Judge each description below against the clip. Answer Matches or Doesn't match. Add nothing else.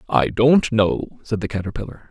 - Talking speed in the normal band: Matches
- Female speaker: Doesn't match